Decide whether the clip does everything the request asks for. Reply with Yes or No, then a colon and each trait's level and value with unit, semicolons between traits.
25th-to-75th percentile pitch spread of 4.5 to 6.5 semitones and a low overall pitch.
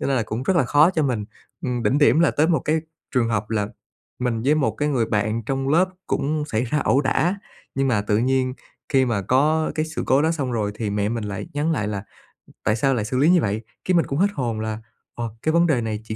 Yes: wide, 5.4 semitones; low, 130 Hz